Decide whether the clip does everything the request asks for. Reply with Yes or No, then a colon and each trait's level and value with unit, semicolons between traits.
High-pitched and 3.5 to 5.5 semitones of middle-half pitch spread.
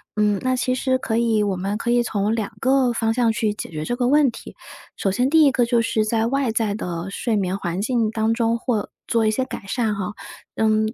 No: high, 225 Hz; average, 2.7 semitones